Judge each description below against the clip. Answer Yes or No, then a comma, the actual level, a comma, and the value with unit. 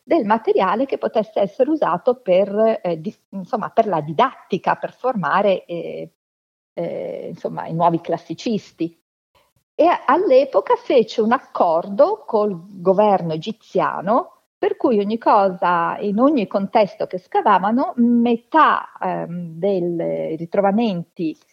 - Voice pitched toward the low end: No, high, 205 Hz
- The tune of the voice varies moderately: No, wide, 6.3 semitones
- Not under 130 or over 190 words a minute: No, average, 120 wpm